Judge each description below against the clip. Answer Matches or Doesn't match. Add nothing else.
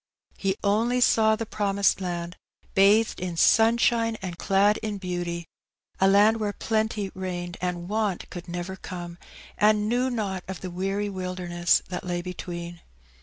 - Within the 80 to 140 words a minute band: Doesn't match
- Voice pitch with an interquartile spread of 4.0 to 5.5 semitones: Doesn't match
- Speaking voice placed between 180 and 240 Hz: Matches